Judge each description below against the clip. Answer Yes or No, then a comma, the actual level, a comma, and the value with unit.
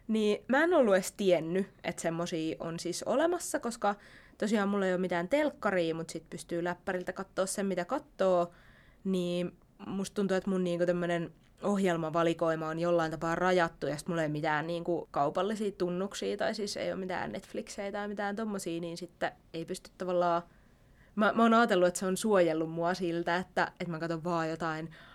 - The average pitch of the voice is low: No, medium, 180 Hz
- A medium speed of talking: No, fast, 185 wpm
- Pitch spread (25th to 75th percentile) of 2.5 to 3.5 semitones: Yes, average, 3.0 semitones